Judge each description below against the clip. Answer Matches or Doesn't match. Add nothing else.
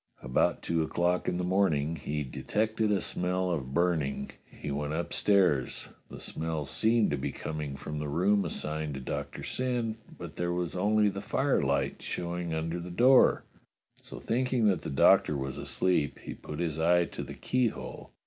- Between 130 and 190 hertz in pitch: Doesn't match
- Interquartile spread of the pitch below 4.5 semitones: Doesn't match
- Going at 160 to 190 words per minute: Matches